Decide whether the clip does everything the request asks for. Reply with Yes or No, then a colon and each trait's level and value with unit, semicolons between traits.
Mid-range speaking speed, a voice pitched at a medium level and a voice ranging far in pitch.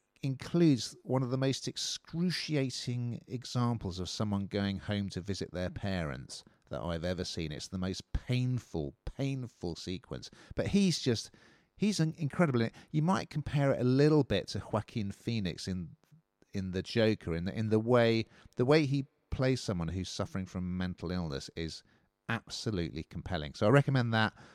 No: average, 165 wpm; low, 110 Hz; wide, 6.1 semitones